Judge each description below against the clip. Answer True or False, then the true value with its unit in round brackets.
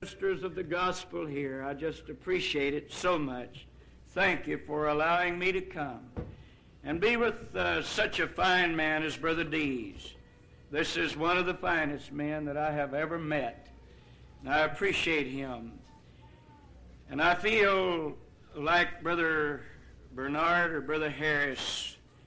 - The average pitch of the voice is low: False (155 Hz)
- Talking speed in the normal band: True (145 wpm)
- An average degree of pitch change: True (3.7 semitones)